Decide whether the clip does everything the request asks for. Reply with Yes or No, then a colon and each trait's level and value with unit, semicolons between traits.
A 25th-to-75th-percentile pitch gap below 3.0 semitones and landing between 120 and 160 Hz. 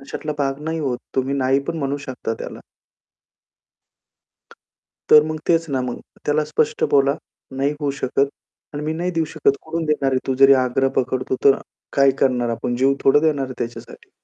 Yes: narrow, 2.5 semitones; medium, 140 Hz